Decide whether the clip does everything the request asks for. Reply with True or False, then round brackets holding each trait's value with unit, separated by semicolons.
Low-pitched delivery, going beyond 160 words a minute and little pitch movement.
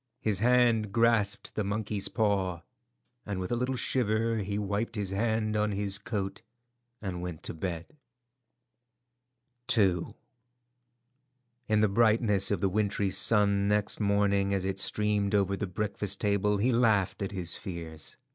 False (100 Hz; 145 wpm; 1.8 semitones)